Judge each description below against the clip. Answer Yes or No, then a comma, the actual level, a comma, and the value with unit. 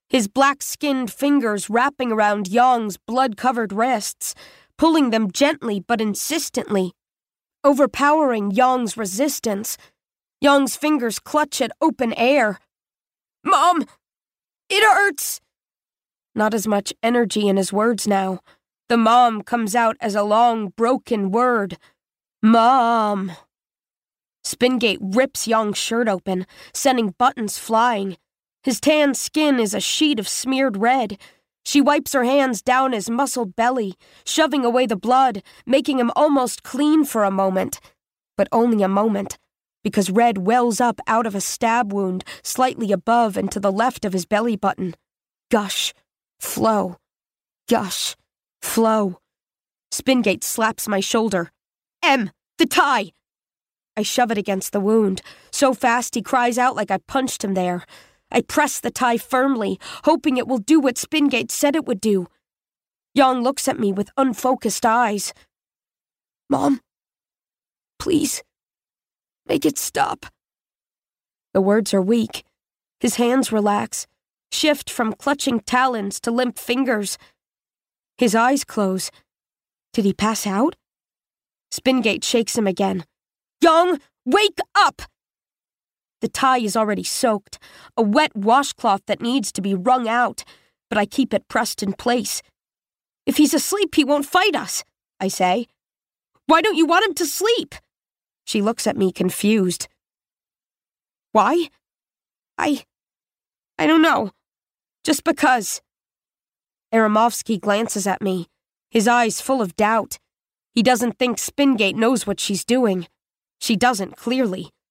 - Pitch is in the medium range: No, high, 235 Hz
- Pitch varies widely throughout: No, average, 4.3 semitones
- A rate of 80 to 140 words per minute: Yes, slow, 135 wpm